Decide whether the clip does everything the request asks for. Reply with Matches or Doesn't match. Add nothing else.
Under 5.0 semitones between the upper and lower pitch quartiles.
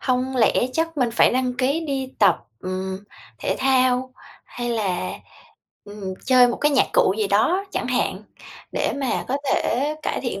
Matches